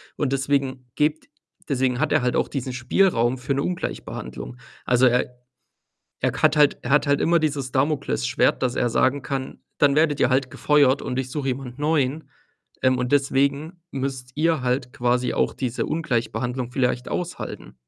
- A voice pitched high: No, low, 135 Hz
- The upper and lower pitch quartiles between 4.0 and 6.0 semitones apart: No, average, 2.7 semitones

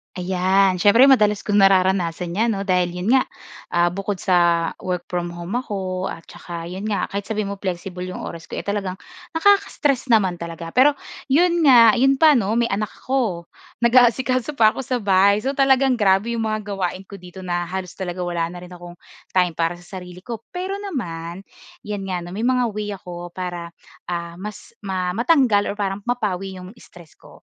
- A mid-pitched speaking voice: No, high, 195 Hz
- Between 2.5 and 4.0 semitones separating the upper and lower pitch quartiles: No, average, 4.4 semitones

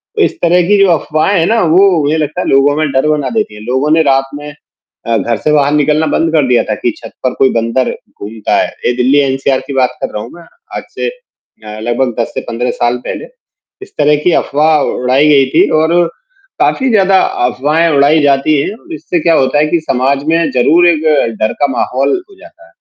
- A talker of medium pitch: Yes, medium, 145 Hz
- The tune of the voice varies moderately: Yes, average, 3.9 semitones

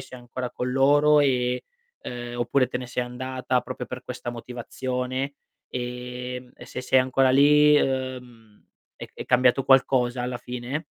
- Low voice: Yes, low, 125 Hz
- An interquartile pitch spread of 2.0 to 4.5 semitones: No, narrow, 1.1 semitones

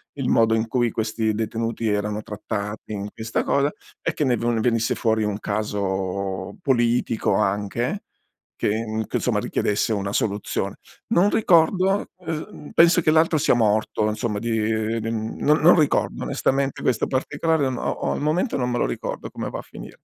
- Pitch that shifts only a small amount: No, average, 4.7 semitones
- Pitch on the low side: Yes, low, 115 Hz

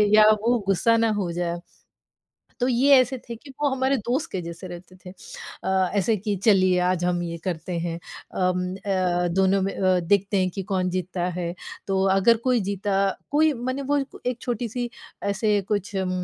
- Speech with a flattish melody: No, average, 4.3 semitones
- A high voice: Yes, high, 195 Hz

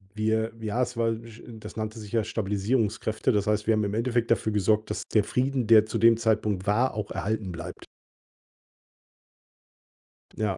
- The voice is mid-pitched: No, low, 110 Hz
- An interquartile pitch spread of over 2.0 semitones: No, narrow, 1.5 semitones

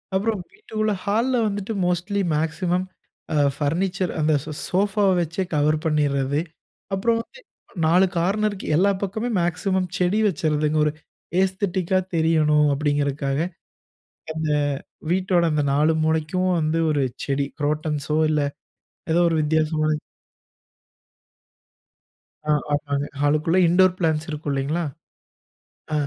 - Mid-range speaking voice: Yes, medium, 165 Hz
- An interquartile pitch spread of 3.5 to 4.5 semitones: Yes, average, 3.9 semitones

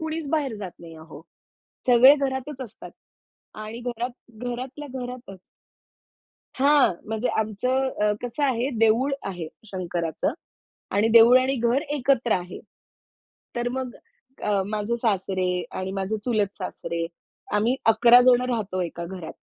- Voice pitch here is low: No, high, 230 Hz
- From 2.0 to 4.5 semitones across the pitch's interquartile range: No, average, 5.0 semitones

